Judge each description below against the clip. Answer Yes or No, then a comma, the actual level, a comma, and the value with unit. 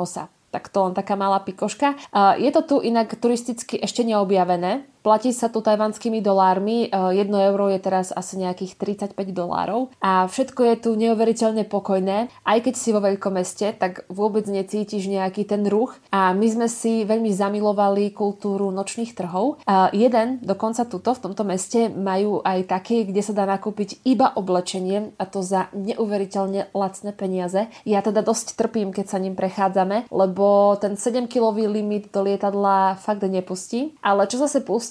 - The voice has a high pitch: Yes, high, 205 Hz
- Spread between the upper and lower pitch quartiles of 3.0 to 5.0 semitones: No, narrow, 2.6 semitones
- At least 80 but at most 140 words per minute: No, fast, 165 wpm